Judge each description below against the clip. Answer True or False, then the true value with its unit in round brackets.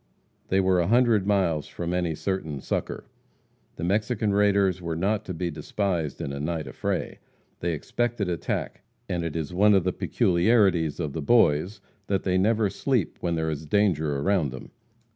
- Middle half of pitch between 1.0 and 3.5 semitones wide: False (4.0 semitones)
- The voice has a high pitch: False (90 Hz)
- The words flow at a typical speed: True (175 wpm)